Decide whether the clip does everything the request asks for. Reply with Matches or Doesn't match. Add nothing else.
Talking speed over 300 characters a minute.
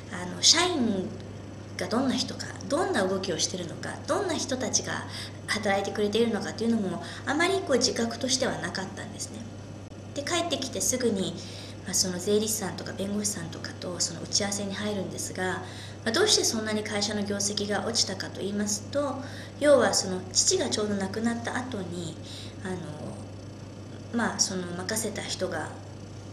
Matches